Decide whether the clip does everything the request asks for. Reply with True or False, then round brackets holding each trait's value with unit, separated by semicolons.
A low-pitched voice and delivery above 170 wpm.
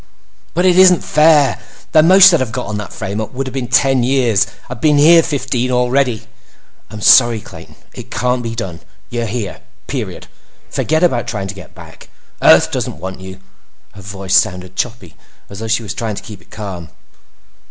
True (120 Hz; 185 wpm)